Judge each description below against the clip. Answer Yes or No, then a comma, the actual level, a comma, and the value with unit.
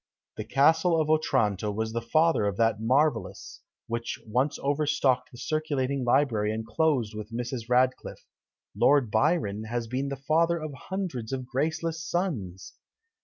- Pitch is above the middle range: No, low, 130 Hz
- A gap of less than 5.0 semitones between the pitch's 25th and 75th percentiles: No, wide, 5.5 semitones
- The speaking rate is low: No, average, 150 wpm